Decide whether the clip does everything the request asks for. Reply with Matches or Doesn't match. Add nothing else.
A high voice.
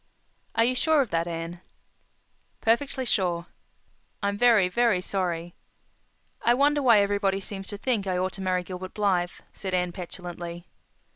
Matches